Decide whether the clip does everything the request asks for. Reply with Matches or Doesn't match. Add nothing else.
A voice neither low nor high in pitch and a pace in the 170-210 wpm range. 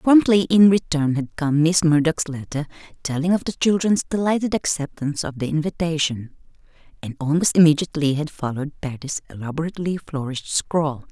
Doesn't match